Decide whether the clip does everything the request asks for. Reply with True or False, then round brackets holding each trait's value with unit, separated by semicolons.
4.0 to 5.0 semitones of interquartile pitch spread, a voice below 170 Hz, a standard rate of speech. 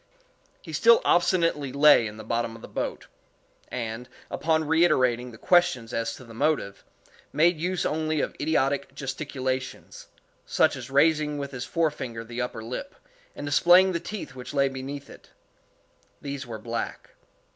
True (4.5 semitones; 140 Hz; 155 wpm)